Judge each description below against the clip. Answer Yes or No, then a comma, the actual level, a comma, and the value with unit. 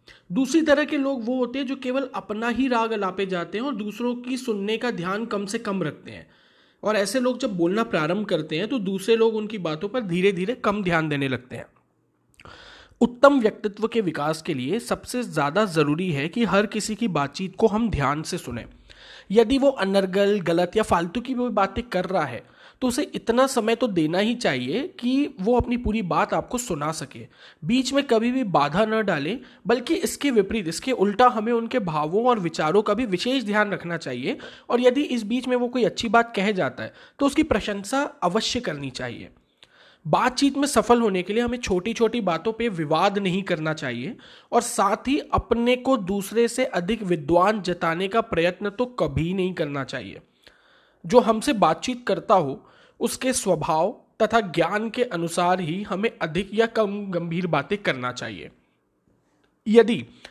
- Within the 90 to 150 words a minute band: No, fast, 190 wpm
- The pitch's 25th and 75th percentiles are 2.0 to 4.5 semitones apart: No, average, 5.3 semitones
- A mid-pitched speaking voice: No, high, 210 Hz